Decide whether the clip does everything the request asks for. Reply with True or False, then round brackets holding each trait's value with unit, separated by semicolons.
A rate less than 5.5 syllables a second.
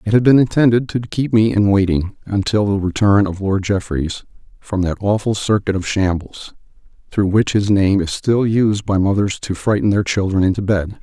True (5.0 syllables/s)